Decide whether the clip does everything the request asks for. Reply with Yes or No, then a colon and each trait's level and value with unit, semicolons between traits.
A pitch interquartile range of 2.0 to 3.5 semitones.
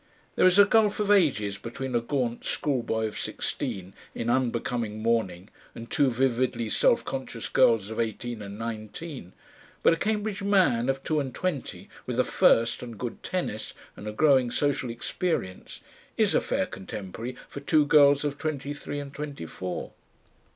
No: average, 4.7 semitones